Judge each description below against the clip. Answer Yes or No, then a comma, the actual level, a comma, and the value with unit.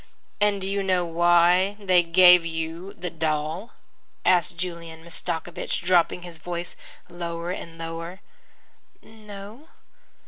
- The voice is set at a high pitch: No, medium, 175 Hz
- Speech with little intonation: Yes, narrow, 1.9 semitones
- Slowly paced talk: Yes, slow, 115 wpm